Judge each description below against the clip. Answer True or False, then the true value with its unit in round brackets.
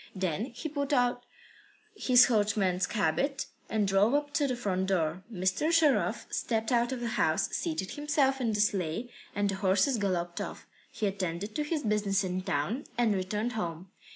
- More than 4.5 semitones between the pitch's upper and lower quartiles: True (5.1 semitones)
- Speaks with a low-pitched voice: False (210 Hz)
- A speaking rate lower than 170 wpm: False (175 wpm)